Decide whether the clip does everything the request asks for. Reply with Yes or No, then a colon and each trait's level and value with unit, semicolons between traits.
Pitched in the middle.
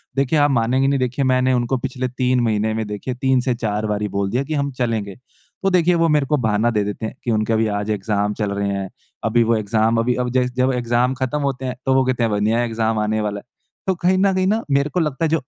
No: low, 125 Hz